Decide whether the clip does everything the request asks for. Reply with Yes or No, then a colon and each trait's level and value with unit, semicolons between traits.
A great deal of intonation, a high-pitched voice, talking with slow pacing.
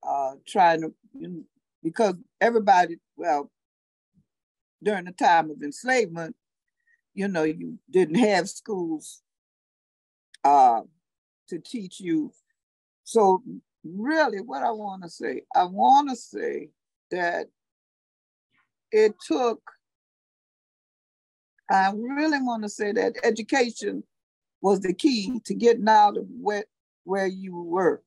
Yes: wide, 7.8 semitones; high, 225 Hz; slow, 120 wpm